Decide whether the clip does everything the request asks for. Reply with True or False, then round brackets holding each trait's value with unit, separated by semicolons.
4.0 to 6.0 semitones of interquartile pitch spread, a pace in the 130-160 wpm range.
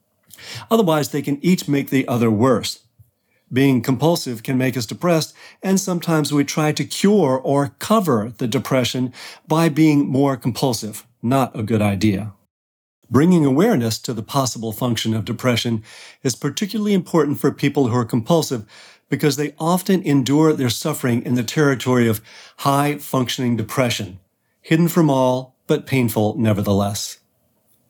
True (4.6 semitones; 145 wpm)